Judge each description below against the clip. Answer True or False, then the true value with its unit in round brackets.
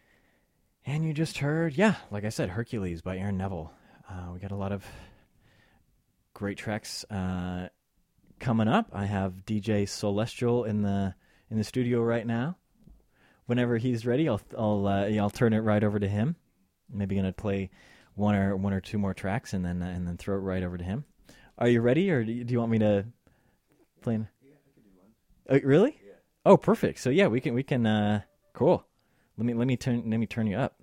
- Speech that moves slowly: False (200 wpm)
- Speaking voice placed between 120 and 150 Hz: False (105 Hz)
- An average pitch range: True (3.5 semitones)